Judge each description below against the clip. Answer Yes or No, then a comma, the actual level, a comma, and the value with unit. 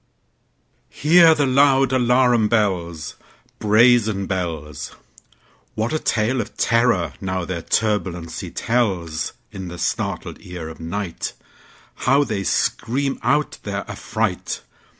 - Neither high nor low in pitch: No, low, 105 Hz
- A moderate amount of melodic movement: No, wide, 5.9 semitones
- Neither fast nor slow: No, slow, 95 wpm